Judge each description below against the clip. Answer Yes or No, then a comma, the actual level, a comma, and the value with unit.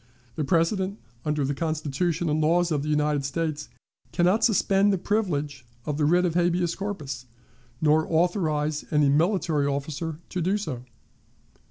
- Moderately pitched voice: Yes, medium, 160 Hz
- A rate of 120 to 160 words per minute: Yes, average, 155 wpm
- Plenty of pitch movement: No, average, 3.1 semitones